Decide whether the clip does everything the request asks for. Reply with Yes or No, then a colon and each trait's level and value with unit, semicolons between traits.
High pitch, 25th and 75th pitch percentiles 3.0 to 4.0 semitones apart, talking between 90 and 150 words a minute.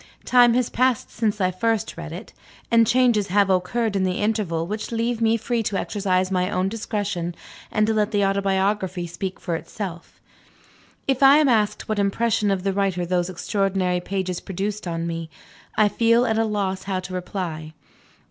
No: high, 200 Hz; average, 3.3 semitones; average, 180 wpm